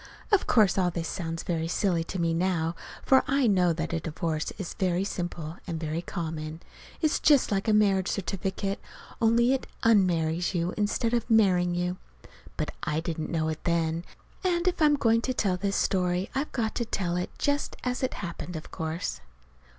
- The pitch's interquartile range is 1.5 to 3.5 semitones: No, average, 4.9 semitones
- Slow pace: No, average, 185 wpm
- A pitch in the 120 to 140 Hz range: No, medium, 180 Hz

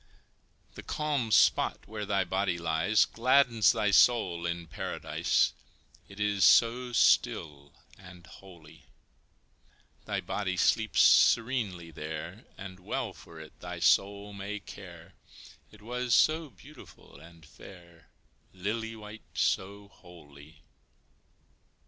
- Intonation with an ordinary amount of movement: Yes, average, 4.3 semitones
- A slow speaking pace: Yes, slow, 110 wpm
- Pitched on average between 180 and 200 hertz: No, very low, 95 Hz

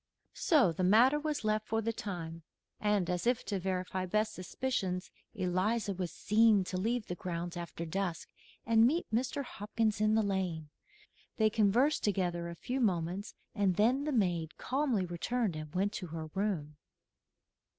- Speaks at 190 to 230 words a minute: No, average, 160 wpm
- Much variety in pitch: No, average, 4.1 semitones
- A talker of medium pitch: No, high, 200 Hz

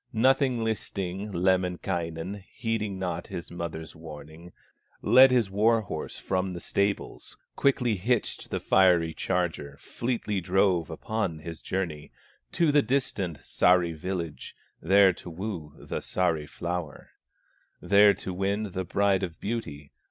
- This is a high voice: No, very low, 95 Hz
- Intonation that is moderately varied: Yes, average, 3.8 semitones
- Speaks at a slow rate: Yes, slow, 130 wpm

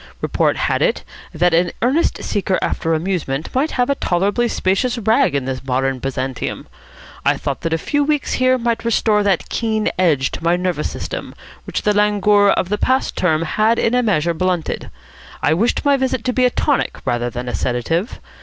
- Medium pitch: No, high, 195 Hz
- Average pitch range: No, wide, 6.9 semitones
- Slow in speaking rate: No, average, 190 wpm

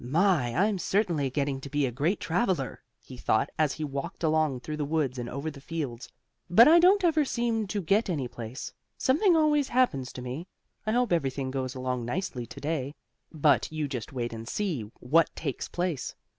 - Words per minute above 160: Yes, average, 200 wpm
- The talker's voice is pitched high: No, medium, 150 Hz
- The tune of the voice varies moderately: No, wide, 6.8 semitones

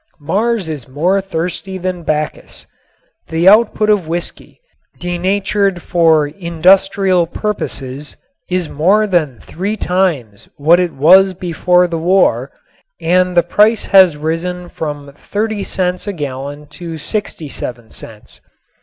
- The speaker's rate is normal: No, slow, 120 wpm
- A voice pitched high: No, medium, 175 Hz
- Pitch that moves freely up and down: No, average, 3.8 semitones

